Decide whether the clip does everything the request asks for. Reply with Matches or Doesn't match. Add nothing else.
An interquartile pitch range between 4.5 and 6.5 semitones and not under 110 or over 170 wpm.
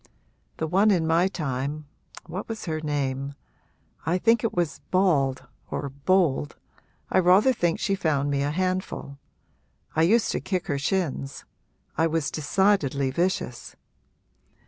Matches